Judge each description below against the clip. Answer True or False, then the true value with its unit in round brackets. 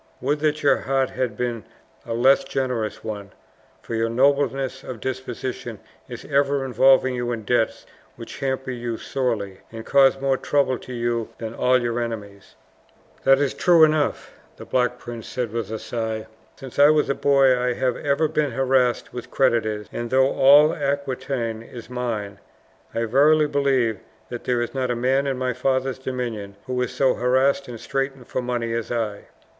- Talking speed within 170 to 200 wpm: True (175 wpm)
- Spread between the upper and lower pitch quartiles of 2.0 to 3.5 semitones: True (2.6 semitones)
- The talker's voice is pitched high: False (125 Hz)